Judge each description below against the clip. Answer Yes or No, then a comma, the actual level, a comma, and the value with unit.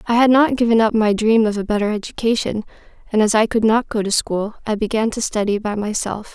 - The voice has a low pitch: No, high, 220 Hz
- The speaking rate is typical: No, fast, 235 wpm